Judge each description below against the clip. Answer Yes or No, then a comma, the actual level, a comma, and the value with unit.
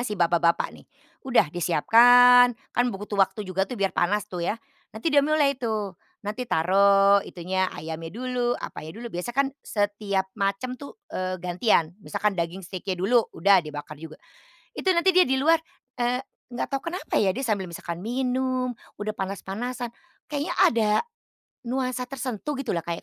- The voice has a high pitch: Yes, high, 210 Hz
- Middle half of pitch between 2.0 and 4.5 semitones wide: No, average, 5.2 semitones